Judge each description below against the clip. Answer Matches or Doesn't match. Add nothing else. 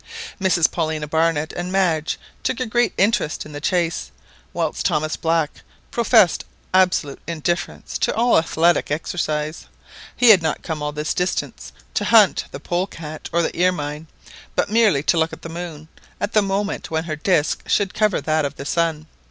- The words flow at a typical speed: Matches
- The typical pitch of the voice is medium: Matches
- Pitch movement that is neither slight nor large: Matches